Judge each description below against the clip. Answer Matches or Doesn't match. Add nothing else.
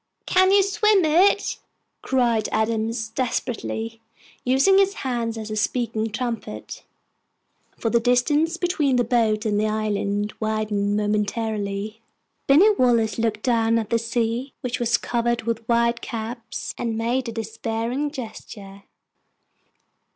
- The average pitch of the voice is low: Doesn't match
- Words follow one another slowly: Matches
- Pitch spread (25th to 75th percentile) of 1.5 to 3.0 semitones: Matches